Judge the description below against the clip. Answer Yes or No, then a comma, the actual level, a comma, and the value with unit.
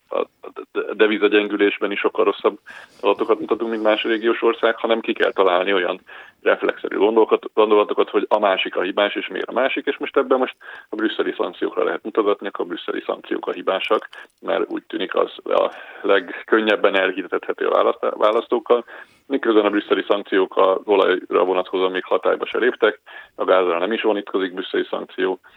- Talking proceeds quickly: Yes, fast, 160 wpm